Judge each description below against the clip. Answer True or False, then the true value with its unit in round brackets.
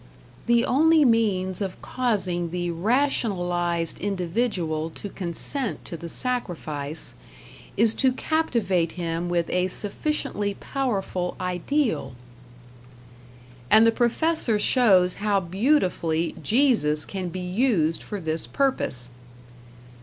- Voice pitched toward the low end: False (190 Hz)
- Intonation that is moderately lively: False (5.7 semitones)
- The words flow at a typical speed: False (105 wpm)